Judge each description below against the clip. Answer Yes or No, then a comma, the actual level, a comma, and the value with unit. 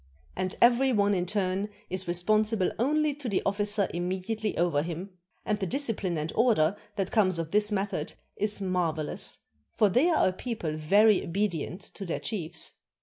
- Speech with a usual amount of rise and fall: Yes, average, 3.5 semitones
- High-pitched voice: Yes, high, 195 Hz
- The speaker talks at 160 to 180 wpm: Yes, average, 170 wpm